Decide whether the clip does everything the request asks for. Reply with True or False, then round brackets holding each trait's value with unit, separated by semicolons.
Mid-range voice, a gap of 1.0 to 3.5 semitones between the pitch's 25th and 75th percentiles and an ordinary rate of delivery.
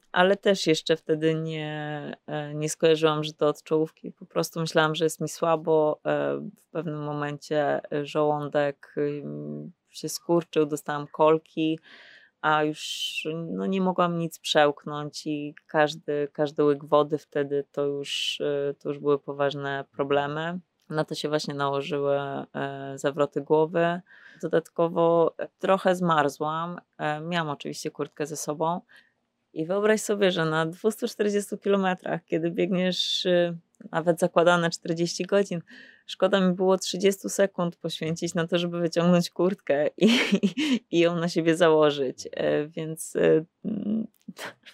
True (160 Hz; 3.0 semitones; 130 wpm)